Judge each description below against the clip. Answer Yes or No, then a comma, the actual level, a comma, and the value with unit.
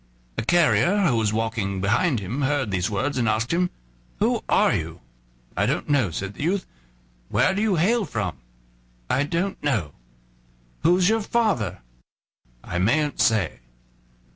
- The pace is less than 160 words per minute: Yes, average, 150 wpm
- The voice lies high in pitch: No, low, 130 Hz